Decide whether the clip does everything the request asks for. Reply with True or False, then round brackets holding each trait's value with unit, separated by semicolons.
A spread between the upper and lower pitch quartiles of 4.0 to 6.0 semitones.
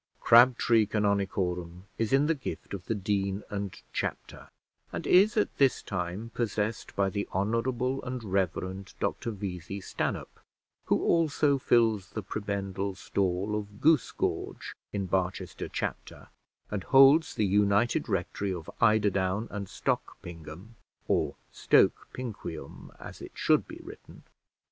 False (3.6 semitones)